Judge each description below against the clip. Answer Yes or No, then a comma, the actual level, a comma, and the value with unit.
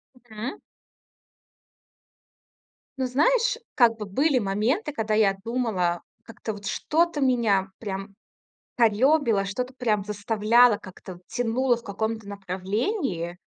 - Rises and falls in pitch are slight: No, average, 4.0 semitones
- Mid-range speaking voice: No, high, 225 Hz